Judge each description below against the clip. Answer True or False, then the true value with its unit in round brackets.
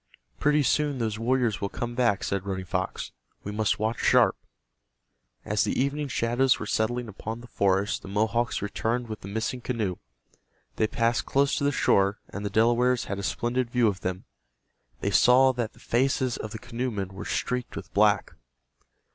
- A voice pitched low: True (115 Hz)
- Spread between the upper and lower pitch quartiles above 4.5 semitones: False (3.3 semitones)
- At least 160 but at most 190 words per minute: True (180 wpm)